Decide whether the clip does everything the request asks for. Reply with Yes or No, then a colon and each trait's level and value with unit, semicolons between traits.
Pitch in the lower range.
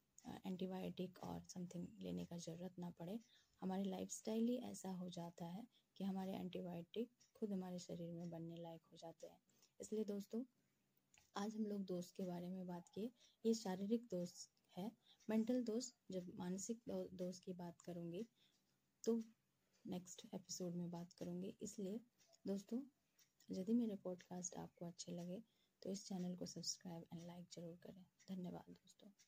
No: medium, 185 Hz